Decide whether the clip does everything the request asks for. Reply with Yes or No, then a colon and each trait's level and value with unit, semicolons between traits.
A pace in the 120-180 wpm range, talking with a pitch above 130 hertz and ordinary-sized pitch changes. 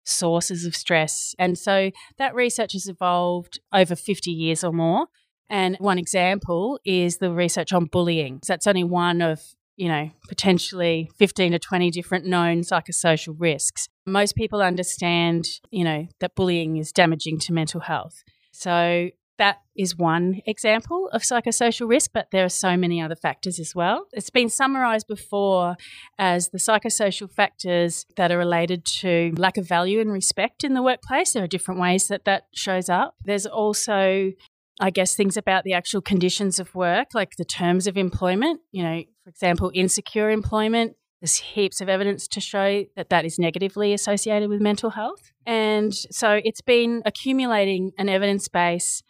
Yes: average, 170 wpm; medium, 185 Hz; average, 3.0 semitones